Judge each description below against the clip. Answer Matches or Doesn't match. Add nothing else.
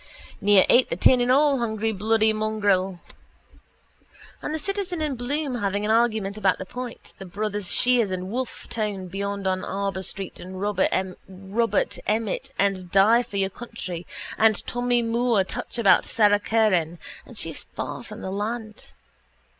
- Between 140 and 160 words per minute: Matches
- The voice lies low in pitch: Doesn't match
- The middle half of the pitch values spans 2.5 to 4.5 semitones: Matches